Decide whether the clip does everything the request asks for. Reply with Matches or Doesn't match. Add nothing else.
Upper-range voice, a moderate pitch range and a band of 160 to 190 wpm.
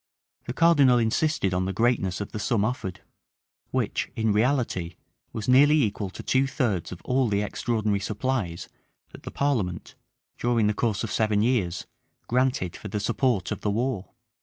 Doesn't match